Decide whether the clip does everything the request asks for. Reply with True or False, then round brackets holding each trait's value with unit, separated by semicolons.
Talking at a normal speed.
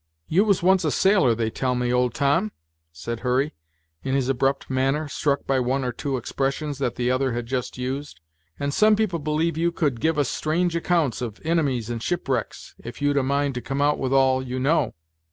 False (210 wpm)